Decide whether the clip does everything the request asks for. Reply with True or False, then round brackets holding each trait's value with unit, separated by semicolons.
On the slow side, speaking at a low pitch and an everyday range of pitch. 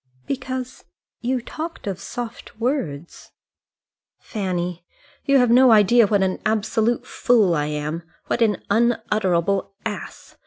False (120 wpm; 215 Hz; 4.6 semitones)